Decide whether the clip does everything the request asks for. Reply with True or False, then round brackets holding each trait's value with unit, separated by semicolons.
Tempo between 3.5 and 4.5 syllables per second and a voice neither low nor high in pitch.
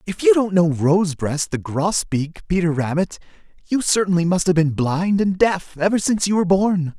False (5.0 syllables/s; 170 Hz)